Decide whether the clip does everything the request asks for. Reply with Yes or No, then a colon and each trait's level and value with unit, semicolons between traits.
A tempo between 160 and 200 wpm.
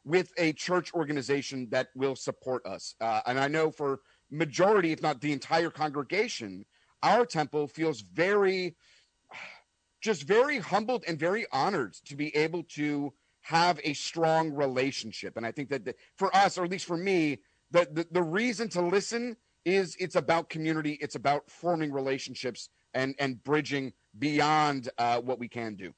Yes: average, 165 wpm